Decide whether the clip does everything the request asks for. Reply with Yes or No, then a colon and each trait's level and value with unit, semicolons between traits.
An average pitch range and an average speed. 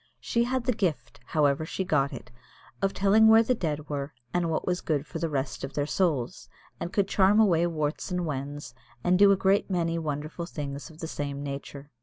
No: average, 4.8 semitones; fast, 210 wpm